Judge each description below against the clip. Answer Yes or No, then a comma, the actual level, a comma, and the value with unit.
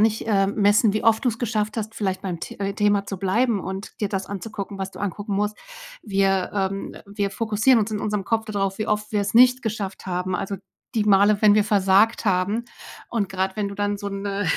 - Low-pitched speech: No, high, 205 Hz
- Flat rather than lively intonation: Yes, narrow, 1.6 semitones